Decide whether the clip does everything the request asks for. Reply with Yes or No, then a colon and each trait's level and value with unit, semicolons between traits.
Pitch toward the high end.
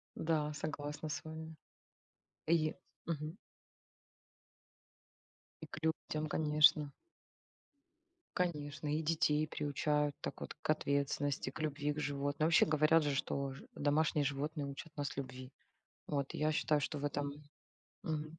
No: medium, 150 Hz